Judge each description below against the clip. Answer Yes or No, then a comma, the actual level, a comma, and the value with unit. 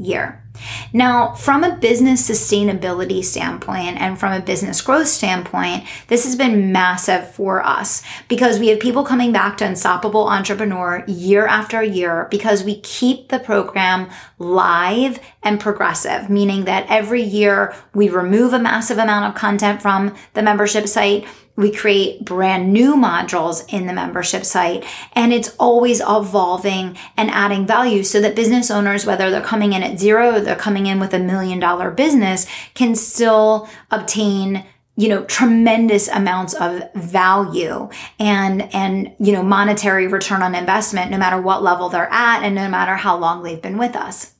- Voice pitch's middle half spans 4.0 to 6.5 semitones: No, average, 2.9 semitones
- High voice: Yes, high, 205 Hz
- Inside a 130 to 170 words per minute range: Yes, average, 165 wpm